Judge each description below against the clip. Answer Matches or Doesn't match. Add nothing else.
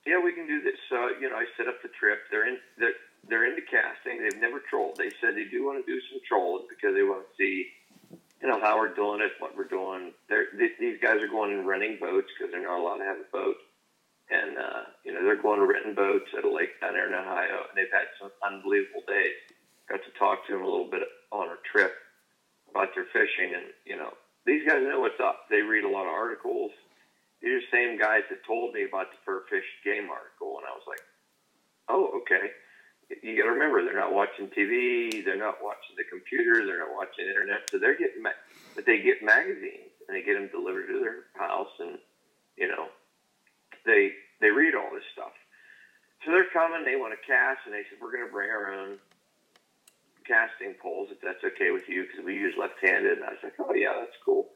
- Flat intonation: Matches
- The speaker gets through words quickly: Matches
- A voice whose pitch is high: Matches